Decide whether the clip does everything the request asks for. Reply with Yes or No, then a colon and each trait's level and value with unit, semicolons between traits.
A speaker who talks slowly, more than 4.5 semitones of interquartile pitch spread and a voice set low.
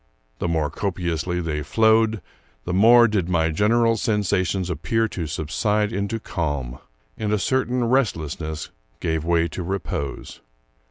Yes: slow, 130 wpm; average, 5.3 semitones; very low, 90 Hz